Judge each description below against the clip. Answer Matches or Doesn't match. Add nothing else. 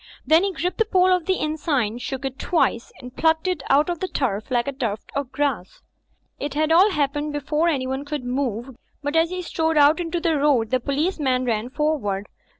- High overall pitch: Matches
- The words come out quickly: Matches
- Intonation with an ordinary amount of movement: Matches